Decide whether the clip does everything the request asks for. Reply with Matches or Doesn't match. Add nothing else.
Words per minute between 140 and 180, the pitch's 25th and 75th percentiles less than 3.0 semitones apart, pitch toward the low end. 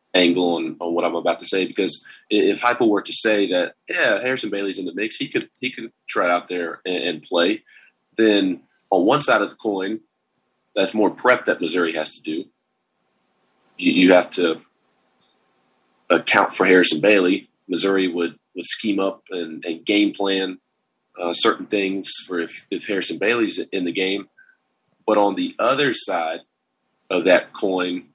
Matches